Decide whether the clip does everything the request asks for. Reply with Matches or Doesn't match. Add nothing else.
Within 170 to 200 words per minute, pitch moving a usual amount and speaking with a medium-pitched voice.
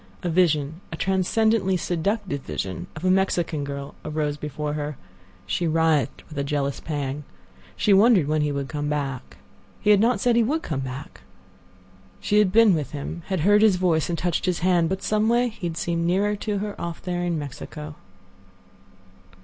Matches